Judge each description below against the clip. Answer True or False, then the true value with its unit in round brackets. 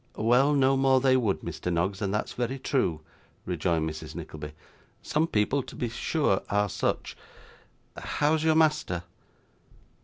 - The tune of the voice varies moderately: False (7.2 semitones)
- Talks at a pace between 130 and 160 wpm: True (145 wpm)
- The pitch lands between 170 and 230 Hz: False (120 Hz)